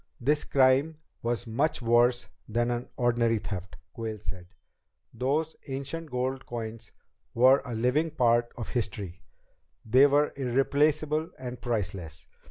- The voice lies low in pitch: Yes, low, 125 Hz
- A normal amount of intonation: Yes, average, 3.3 semitones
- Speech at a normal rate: No, slow, 125 wpm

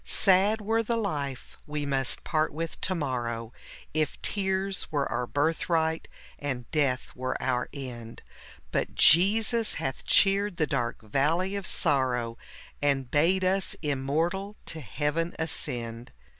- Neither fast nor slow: No, slow, 130 wpm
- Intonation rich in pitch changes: Yes, wide, 6.2 semitones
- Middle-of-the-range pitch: Yes, medium, 150 Hz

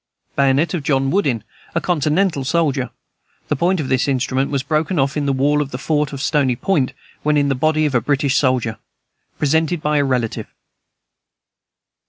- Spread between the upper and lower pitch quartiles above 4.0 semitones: No, narrow, 2.5 semitones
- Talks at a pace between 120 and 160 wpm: No, average, 180 wpm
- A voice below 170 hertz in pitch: Yes, medium, 140 Hz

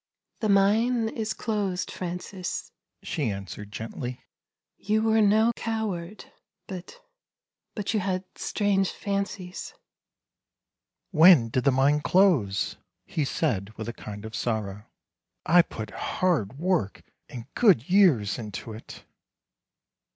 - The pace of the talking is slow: Yes, slow, 130 wpm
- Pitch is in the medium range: Yes, medium, 180 Hz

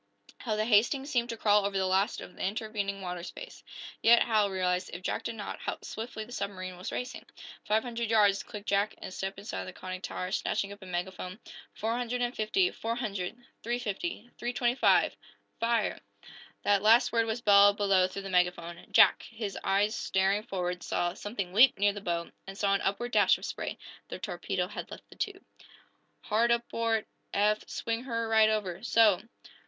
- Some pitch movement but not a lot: Yes, average, 3.2 semitones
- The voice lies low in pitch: No, high, 210 Hz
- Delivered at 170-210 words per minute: Yes, average, 190 wpm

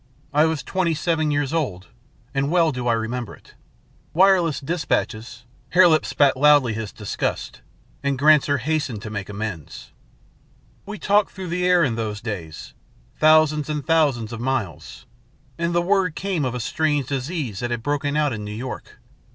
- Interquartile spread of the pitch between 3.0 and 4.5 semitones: No, wide, 5.5 semitones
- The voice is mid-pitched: Yes, medium, 145 Hz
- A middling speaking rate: Yes, average, 170 wpm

